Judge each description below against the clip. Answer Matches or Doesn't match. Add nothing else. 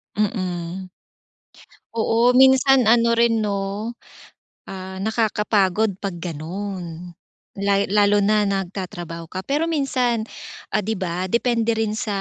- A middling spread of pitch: Matches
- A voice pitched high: Matches